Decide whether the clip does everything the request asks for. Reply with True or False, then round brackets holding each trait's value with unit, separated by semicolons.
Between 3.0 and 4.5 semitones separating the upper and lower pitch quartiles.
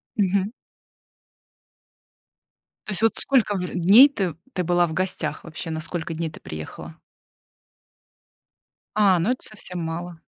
True (3.7 semitones)